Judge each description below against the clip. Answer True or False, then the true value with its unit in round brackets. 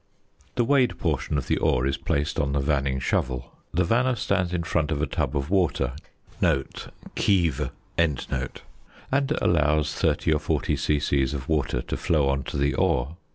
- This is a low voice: True (75 Hz)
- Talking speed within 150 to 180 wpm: True (165 wpm)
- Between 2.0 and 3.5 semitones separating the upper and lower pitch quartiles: False (4.0 semitones)